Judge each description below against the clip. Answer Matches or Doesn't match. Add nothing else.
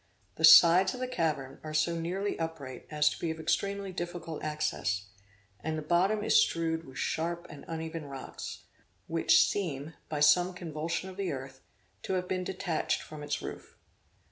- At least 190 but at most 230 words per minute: Doesn't match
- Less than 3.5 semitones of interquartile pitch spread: Matches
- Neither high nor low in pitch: Matches